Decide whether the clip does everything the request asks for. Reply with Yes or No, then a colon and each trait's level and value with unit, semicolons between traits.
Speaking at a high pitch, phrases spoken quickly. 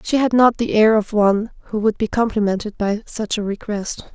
Yes: high, 215 Hz; fast, 215 wpm